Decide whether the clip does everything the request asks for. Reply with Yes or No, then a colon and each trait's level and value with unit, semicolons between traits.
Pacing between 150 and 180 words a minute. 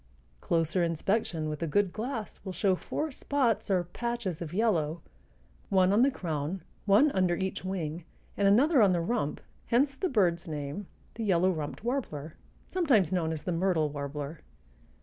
Yes: average, 165 wpm